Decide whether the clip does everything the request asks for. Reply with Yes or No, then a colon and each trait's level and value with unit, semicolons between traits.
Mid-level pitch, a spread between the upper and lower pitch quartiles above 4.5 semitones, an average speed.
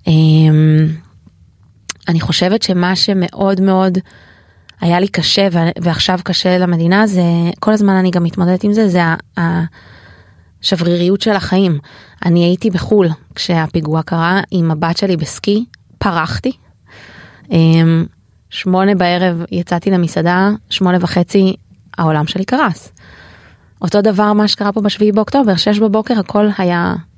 No: medium, 175 Hz; average, 3.3 semitones; average, 120 wpm